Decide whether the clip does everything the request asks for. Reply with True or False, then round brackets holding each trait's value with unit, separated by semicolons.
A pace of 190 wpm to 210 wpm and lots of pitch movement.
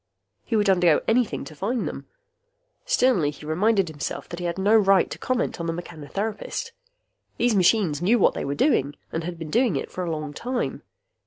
True (195 wpm; 6.0 semitones)